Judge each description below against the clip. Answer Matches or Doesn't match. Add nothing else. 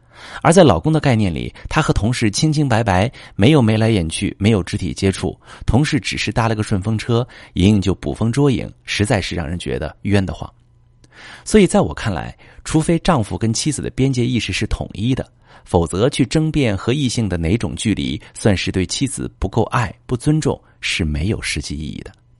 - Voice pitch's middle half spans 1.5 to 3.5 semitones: Doesn't match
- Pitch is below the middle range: Matches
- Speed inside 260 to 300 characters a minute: Matches